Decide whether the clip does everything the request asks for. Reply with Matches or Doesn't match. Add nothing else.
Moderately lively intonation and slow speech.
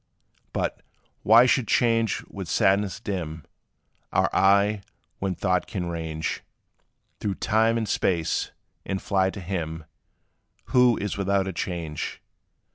Matches